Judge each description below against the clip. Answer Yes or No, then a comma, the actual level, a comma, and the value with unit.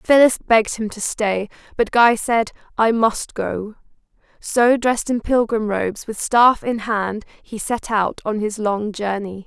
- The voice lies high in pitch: Yes, high, 220 Hz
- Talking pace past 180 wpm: No, average, 170 wpm